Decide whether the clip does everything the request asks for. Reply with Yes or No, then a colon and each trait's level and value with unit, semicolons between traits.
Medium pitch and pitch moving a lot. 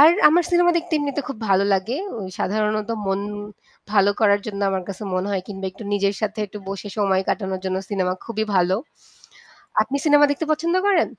No: high, 205 Hz; wide, 6.5 semitones